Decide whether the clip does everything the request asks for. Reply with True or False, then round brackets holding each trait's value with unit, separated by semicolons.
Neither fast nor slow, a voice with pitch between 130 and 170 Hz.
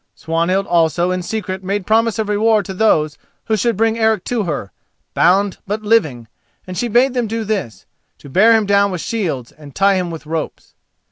False (190 wpm; 200 Hz)